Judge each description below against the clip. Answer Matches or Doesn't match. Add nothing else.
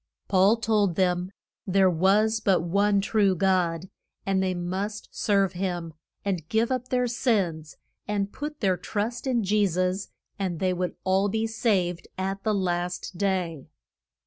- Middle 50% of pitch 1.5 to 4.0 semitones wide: Matches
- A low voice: Doesn't match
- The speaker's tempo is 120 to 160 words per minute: Matches